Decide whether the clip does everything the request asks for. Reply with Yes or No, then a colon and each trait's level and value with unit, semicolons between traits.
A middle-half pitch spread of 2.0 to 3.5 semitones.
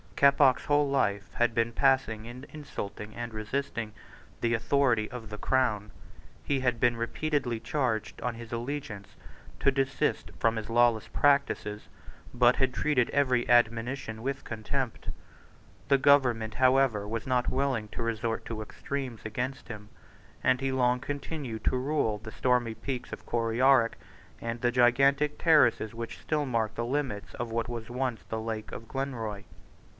Yes: average, 3.1 semitones